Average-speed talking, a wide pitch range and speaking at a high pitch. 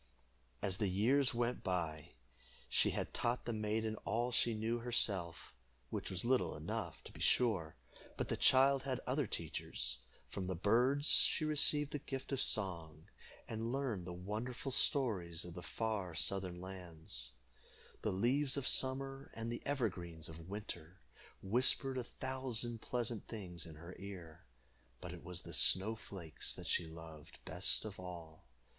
No: average, 155 wpm; wide, 6.2 semitones; low, 105 Hz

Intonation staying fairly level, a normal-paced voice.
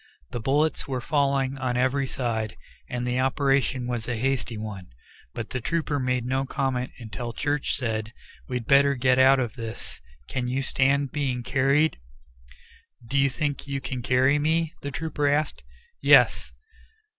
Yes: narrow, 2.3 semitones; average, 155 wpm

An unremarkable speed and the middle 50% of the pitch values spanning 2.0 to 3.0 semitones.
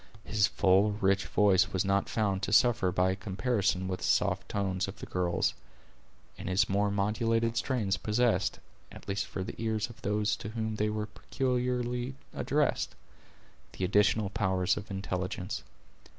Yes: average, 160 wpm; average, 2.7 semitones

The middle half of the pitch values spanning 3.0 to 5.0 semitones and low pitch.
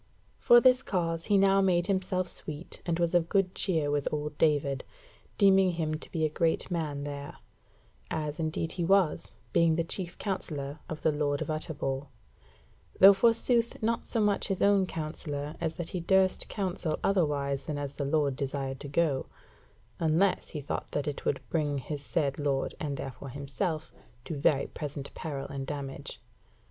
No: average, 4.1 semitones; medium, 155 Hz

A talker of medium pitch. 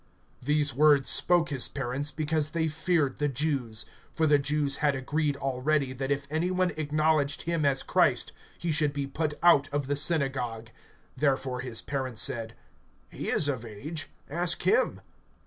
Yes: medium, 145 Hz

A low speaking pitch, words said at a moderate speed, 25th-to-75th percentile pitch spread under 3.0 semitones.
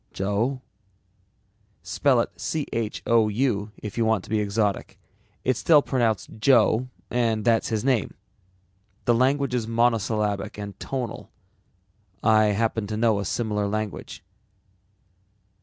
No: low, 110 Hz; slow, 120 wpm; narrow, 2.6 semitones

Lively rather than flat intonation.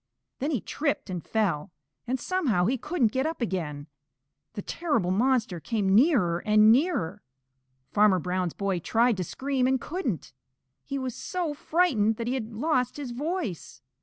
Yes: wide, 6.4 semitones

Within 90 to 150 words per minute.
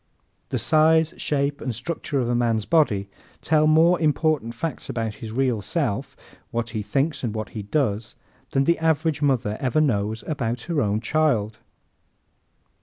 No: average, 160 wpm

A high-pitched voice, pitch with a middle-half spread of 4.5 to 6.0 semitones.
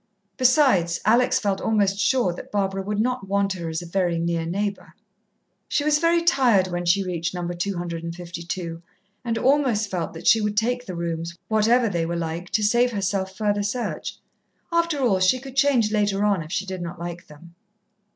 Yes: high, 195 Hz; average, 4.9 semitones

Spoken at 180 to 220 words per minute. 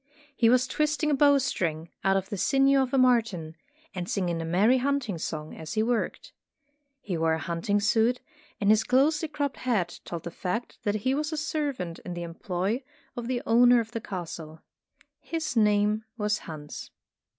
Yes: average, 185 wpm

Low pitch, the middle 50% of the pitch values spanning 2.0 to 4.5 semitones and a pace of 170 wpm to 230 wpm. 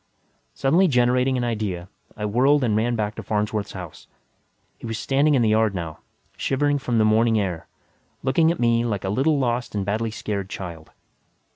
Yes: low, 115 Hz; average, 3.8 semitones; average, 180 wpm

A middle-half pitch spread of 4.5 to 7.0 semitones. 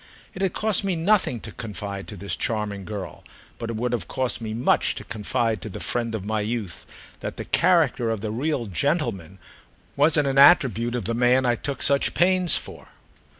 Yes: average, 4.8 semitones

